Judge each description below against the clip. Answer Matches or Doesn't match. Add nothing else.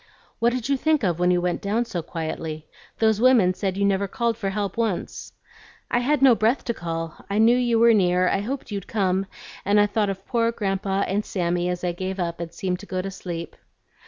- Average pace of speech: Doesn't match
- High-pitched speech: Matches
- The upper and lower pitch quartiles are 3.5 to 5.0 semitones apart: Matches